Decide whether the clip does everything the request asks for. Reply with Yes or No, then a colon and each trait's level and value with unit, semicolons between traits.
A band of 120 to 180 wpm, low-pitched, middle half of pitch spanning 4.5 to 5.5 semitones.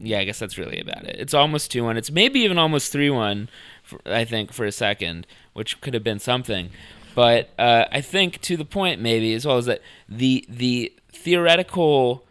No: fast, 205 wpm; low, 120 Hz; average, 5.2 semitones